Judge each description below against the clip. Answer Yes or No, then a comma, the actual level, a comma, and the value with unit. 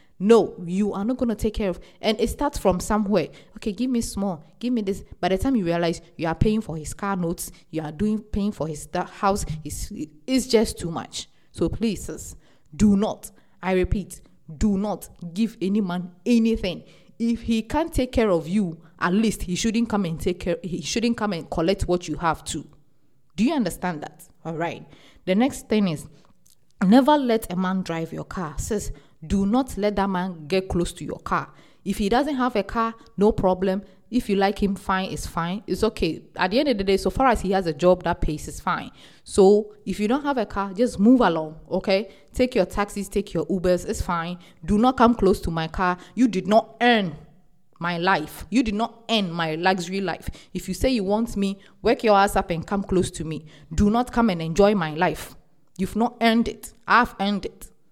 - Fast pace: Yes, fast, 220 wpm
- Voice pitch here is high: Yes, high, 195 Hz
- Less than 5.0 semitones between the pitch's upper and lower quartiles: Yes, average, 4.1 semitones